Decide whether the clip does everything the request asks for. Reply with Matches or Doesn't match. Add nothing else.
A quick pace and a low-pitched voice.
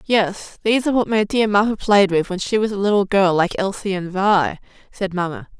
Doesn't match